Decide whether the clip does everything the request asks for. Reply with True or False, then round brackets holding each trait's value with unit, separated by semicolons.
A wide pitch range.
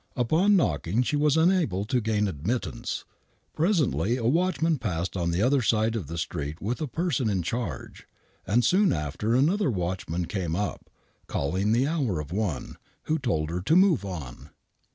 True (8.9 semitones)